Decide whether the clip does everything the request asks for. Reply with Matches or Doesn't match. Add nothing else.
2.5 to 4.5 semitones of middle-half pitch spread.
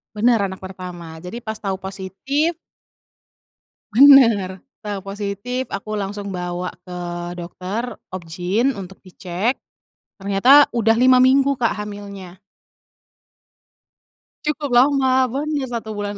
Doesn't match